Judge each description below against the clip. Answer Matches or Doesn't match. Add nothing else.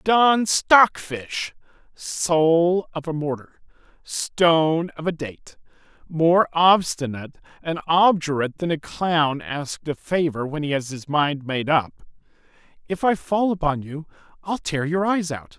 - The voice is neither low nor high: Matches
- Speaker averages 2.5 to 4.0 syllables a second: Matches